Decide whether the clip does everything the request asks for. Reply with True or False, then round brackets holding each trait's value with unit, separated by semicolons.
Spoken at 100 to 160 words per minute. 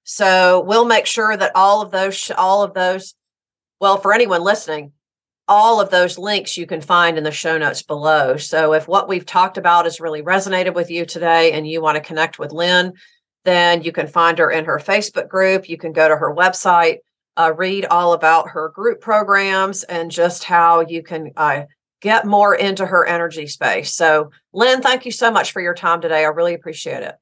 False (205 wpm)